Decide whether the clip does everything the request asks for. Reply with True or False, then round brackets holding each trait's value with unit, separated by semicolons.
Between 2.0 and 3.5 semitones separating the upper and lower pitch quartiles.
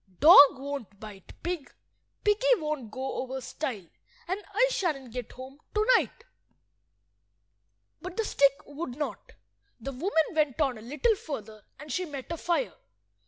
False (5.5 semitones)